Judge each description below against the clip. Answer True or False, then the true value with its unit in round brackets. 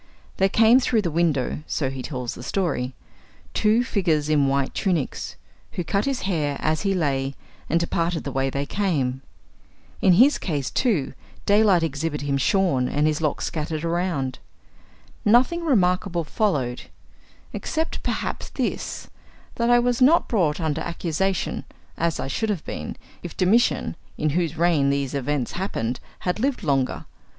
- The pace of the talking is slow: False (155 wpm)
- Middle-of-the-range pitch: True (165 Hz)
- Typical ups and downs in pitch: False (6.0 semitones)